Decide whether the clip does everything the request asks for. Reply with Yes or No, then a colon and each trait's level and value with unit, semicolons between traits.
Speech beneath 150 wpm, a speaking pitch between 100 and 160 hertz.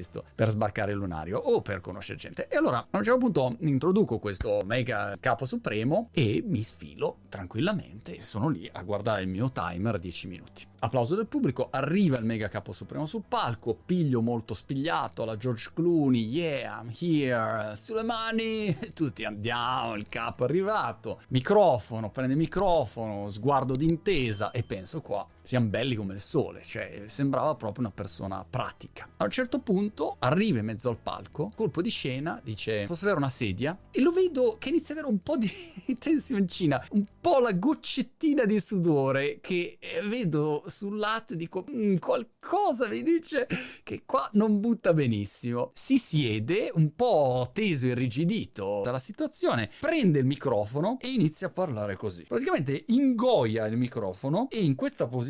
No: average, 165 wpm; medium, 140 Hz